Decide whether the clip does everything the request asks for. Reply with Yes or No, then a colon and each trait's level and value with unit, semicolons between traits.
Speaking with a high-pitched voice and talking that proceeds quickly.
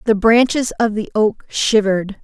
No: high, 215 Hz; average, 160 wpm